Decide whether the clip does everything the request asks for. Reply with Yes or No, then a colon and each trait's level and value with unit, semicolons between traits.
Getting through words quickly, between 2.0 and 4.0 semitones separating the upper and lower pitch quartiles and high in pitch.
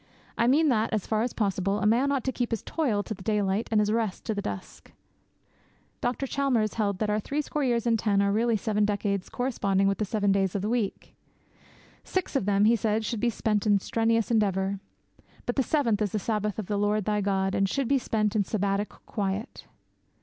Yes: fast, 220 wpm; narrow, 2.6 semitones; high, 215 Hz